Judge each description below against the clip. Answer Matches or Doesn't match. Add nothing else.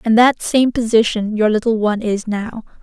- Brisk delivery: Doesn't match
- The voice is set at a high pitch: Matches